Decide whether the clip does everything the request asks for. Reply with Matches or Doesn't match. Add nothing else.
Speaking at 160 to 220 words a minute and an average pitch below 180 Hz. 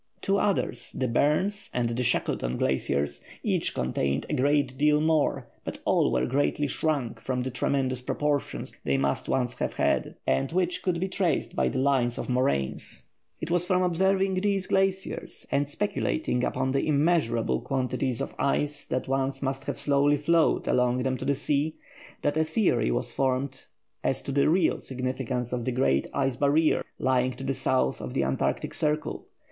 Matches